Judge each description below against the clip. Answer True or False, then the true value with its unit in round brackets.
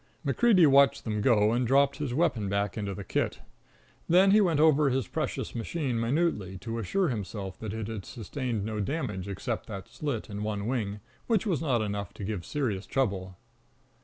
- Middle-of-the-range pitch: False (115 Hz)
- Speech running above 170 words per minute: True (185 wpm)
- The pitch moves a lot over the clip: True (5.7 semitones)